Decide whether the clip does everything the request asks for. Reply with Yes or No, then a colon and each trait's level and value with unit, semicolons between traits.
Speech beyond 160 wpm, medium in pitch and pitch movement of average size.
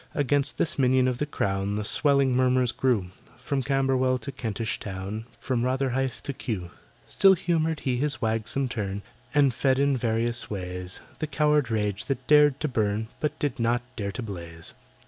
No: average, 170 wpm; low, 125 Hz; average, 4.4 semitones